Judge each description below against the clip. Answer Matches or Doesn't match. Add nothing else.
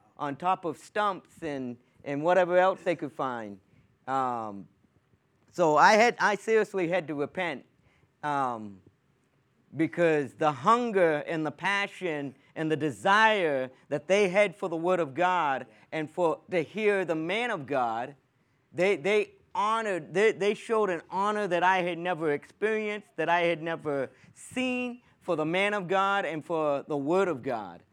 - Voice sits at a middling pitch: Matches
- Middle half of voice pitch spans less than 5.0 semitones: Doesn't match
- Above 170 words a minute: Doesn't match